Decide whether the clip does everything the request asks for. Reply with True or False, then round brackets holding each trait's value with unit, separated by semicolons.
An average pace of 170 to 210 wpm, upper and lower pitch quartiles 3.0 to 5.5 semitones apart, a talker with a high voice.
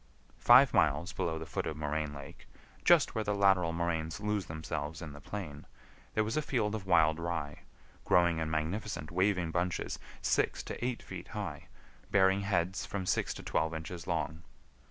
False (175 wpm; 4.0 semitones; 85 Hz)